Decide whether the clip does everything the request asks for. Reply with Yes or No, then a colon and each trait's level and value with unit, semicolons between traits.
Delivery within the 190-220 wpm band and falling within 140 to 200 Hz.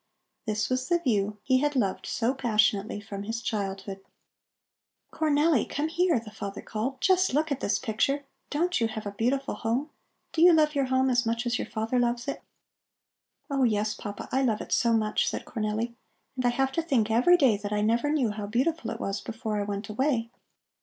No: average, 200 wpm; high, 235 Hz